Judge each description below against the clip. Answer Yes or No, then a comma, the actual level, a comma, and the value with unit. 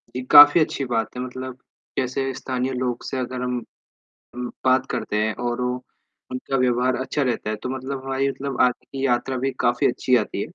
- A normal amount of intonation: No, narrow, 1.2 semitones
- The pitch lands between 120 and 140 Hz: Yes, low, 130 Hz